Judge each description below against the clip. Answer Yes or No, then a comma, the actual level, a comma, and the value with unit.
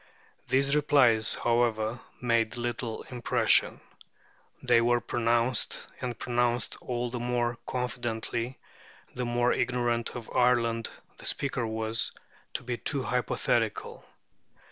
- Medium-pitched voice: No, low, 120 Hz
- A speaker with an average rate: No, slow, 110 wpm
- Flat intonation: Yes, narrow, 1.1 semitones